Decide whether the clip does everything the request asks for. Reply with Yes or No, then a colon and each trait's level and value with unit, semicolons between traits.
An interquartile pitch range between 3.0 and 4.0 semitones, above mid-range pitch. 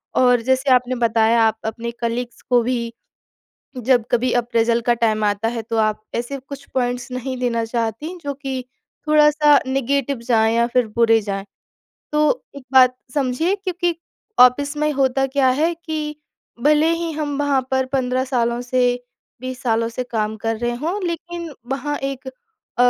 Yes: average, 3.3 semitones; very high, 255 Hz